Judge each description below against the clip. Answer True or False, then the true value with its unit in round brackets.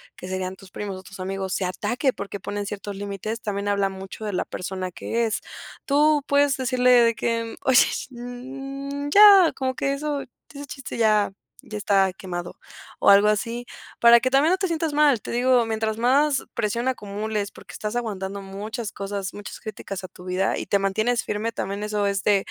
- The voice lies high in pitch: True (215 Hz)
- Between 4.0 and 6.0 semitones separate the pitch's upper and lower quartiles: True (4.5 semitones)